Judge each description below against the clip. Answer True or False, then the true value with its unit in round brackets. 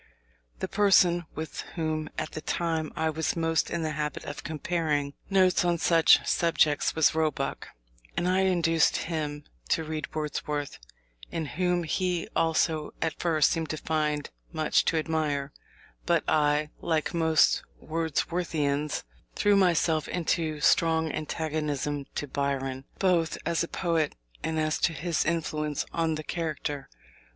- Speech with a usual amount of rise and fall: False (1.8 semitones)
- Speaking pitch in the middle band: True (160 Hz)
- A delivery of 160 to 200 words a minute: False (140 wpm)